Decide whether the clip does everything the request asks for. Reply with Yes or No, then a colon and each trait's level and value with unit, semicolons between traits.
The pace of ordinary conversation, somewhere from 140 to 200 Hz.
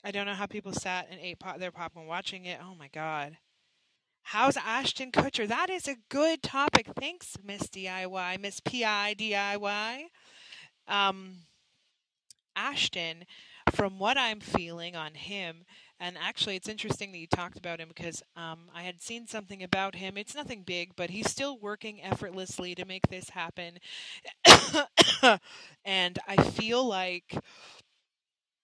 Yes: average, 145 wpm; high, 190 Hz